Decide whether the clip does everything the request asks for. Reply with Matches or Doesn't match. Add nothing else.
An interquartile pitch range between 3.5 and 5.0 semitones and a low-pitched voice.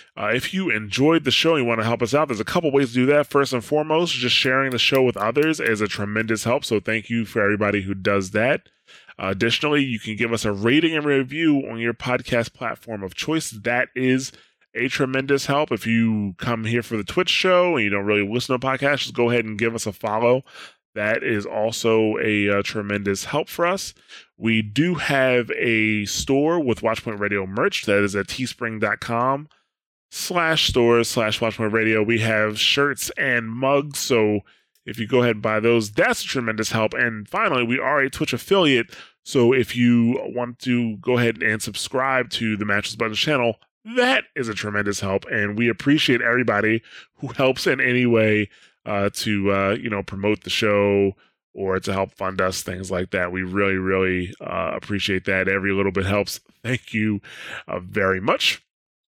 Matches